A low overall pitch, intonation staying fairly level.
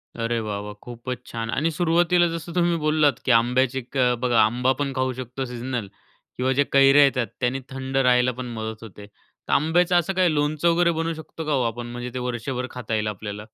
No: low, 130 Hz; average, 4.5 semitones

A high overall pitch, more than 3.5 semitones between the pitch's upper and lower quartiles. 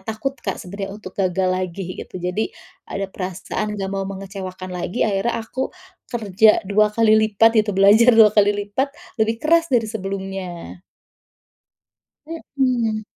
No: high, 200 Hz; narrow, 2.6 semitones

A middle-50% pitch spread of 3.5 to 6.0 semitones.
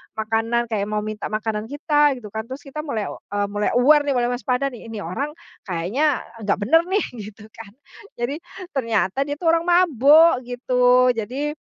Yes: average, 5.0 semitones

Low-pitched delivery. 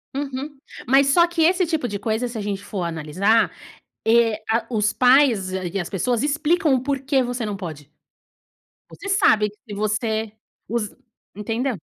No: high, 230 Hz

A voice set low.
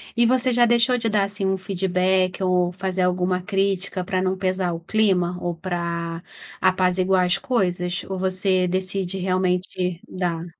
No: medium, 185 Hz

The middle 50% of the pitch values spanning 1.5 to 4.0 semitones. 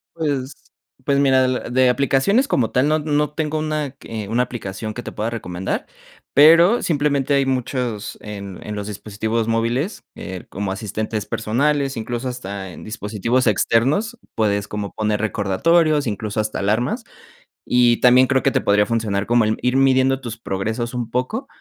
No: average, 4.4 semitones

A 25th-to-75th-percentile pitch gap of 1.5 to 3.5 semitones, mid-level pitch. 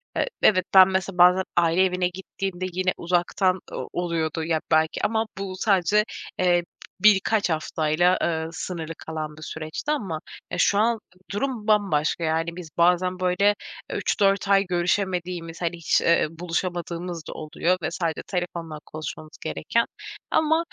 Yes: narrow, 2.6 semitones; medium, 180 Hz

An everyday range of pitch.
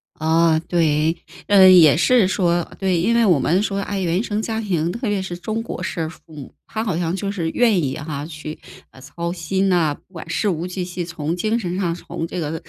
Yes: average, 3.3 semitones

